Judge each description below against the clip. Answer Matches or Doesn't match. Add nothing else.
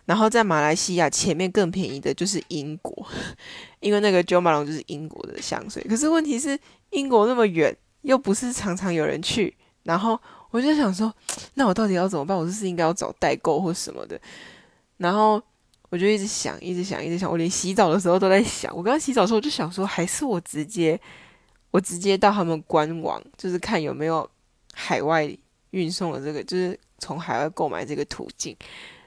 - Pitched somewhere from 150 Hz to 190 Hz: Matches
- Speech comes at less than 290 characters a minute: Doesn't match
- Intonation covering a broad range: Doesn't match